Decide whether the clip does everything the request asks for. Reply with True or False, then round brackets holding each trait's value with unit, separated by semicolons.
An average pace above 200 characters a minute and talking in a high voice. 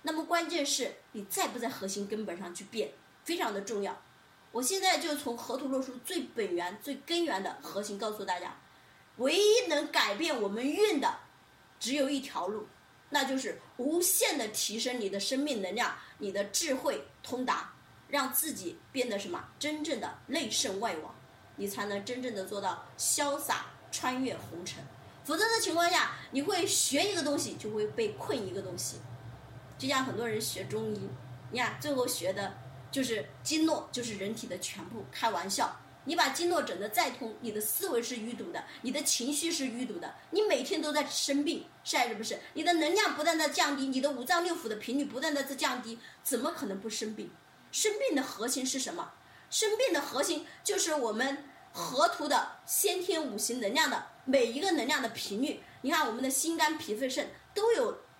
True (275 characters per minute; 275 Hz)